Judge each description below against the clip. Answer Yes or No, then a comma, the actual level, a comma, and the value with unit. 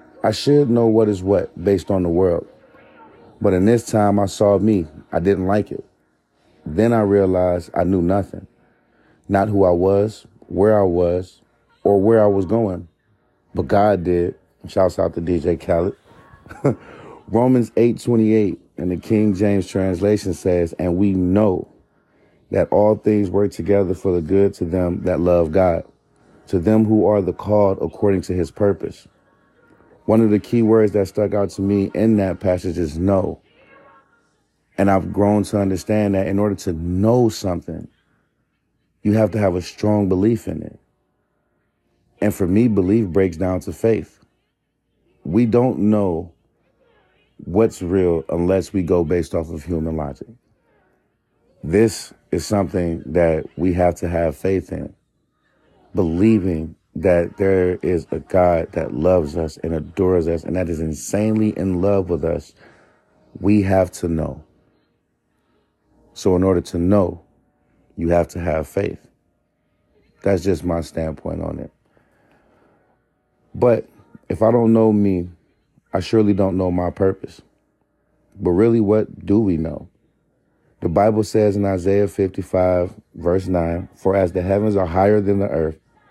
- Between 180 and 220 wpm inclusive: No, average, 155 wpm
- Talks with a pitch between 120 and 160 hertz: No, very low, 95 Hz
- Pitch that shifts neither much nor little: Yes, average, 3.0 semitones